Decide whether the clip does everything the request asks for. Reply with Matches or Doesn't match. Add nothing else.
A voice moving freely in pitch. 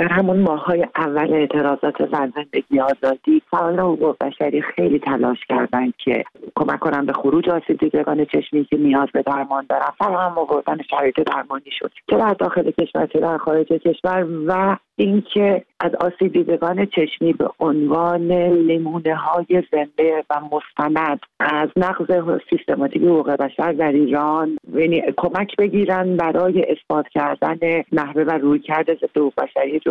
Doesn't match